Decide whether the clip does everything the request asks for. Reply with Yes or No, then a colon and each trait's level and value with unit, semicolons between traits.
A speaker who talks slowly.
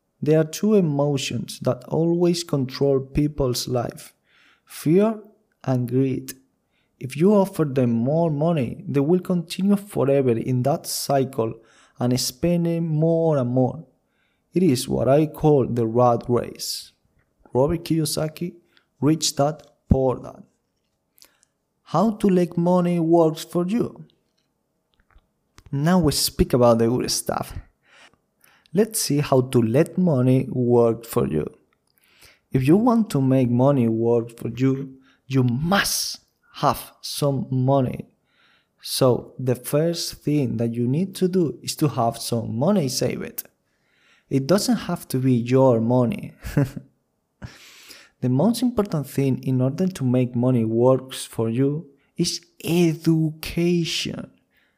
Yes: slow, 130 wpm